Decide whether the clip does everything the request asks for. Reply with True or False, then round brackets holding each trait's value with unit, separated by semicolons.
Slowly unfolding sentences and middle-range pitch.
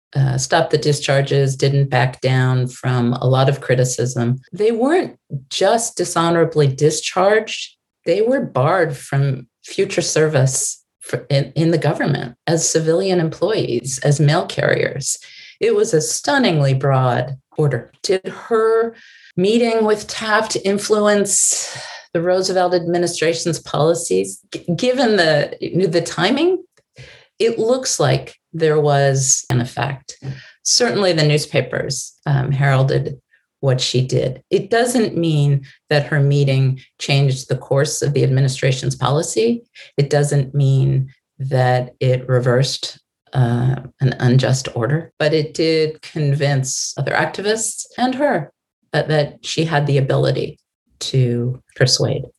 True (125 wpm; 150 Hz)